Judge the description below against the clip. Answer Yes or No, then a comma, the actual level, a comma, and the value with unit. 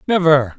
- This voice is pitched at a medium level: Yes, medium, 155 Hz